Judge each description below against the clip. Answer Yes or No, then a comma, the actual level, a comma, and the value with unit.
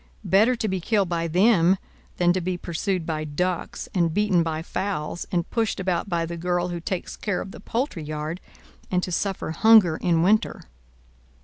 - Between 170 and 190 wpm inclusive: Yes, average, 185 wpm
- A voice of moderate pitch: Yes, medium, 180 Hz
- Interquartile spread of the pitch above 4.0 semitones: No, average, 2.8 semitones